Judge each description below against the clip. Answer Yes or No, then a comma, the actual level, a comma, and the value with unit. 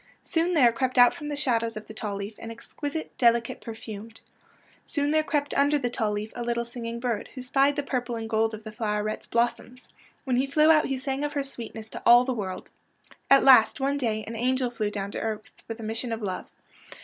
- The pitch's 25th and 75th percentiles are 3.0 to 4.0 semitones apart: Yes, average, 3.6 semitones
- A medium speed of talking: No, fast, 225 wpm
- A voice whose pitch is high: Yes, high, 240 Hz